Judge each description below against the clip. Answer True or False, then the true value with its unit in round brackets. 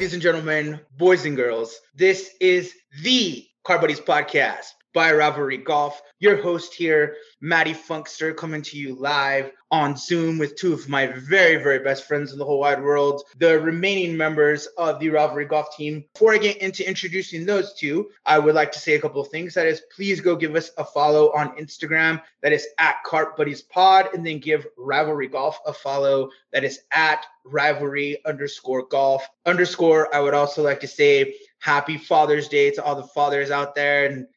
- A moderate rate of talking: True (190 wpm)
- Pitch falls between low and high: True (150 Hz)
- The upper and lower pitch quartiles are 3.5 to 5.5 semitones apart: False (3.1 semitones)